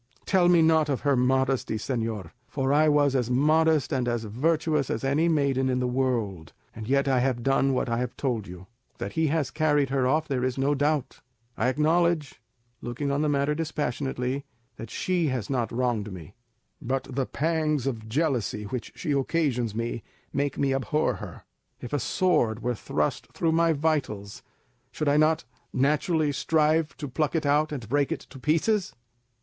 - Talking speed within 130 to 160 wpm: No, average, 180 wpm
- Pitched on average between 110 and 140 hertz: Yes, low, 135 Hz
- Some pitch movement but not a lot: Yes, average, 3.7 semitones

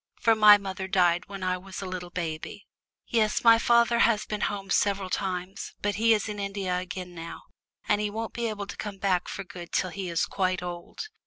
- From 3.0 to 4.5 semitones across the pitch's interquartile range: No, narrow, 2.5 semitones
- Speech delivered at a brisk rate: Yes, fast, 215 wpm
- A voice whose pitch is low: No, high, 195 Hz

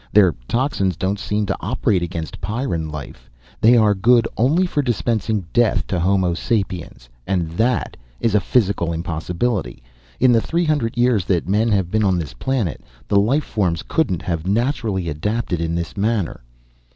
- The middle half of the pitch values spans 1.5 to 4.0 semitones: No, average, 5.3 semitones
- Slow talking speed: No, average, 165 wpm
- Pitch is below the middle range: Yes, low, 100 Hz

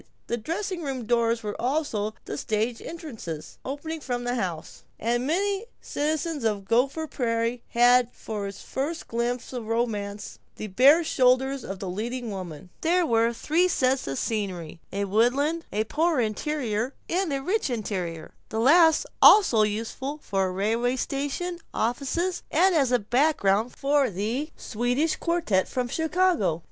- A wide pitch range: Yes, wide, 5.9 semitones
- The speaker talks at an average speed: Yes, average, 150 wpm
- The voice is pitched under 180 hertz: No, high, 245 Hz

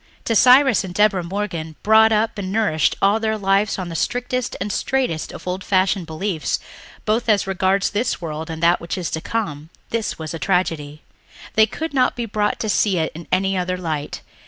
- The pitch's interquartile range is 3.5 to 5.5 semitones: Yes, average, 4.5 semitones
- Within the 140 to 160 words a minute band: No, average, 200 wpm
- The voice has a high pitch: Yes, high, 195 Hz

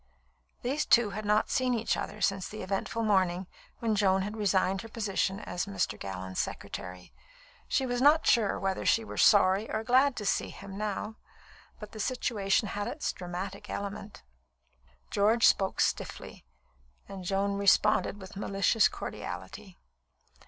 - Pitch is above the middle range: Yes, high, 205 Hz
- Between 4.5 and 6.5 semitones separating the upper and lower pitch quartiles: No, narrow, 2.6 semitones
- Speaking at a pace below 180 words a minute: Yes, average, 150 wpm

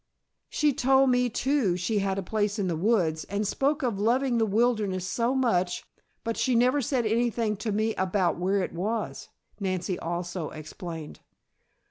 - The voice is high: Yes, high, 210 Hz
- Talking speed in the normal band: Yes, average, 165 wpm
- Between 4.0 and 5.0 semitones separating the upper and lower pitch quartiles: Yes, average, 4.7 semitones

